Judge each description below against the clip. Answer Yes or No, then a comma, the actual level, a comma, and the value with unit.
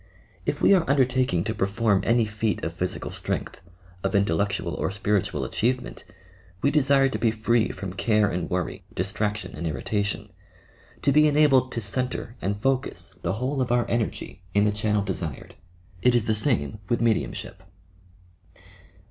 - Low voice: Yes, low, 110 Hz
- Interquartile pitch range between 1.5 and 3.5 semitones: No, average, 4.0 semitones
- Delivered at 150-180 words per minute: Yes, average, 160 wpm